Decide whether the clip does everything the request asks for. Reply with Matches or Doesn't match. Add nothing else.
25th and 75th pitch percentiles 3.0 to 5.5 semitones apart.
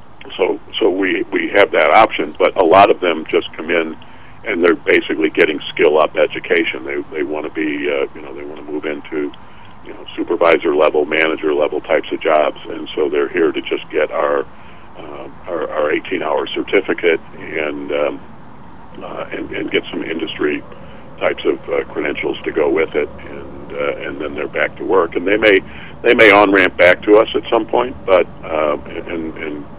Matches